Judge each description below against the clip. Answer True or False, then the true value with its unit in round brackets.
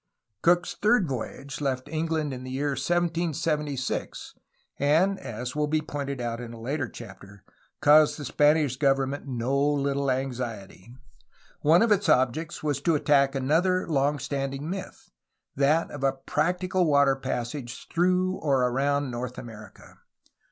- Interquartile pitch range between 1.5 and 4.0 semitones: True (3.4 semitones)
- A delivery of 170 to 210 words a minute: False (145 wpm)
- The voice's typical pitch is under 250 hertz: True (140 Hz)